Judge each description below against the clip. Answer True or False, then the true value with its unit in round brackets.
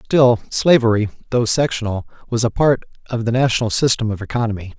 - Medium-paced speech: True (165 wpm)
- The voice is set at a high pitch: False (120 Hz)